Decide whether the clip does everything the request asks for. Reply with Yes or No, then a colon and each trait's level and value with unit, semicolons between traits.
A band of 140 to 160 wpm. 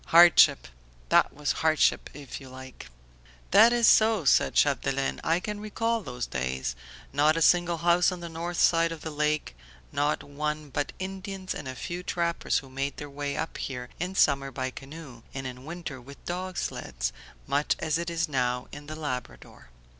No: average, 180 wpm